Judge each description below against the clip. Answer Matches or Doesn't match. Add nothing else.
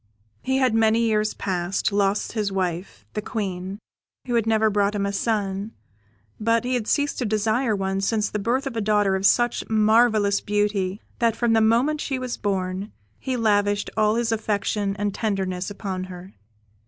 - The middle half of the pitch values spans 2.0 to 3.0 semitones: Matches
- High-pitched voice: Matches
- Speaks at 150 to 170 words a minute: Doesn't match